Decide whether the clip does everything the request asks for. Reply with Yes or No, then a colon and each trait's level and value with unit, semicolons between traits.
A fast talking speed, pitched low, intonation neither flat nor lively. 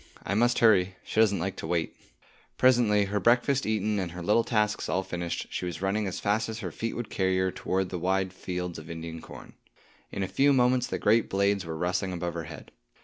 Yes: fast, 220 wpm; very low, 95 Hz; average, 3.5 semitones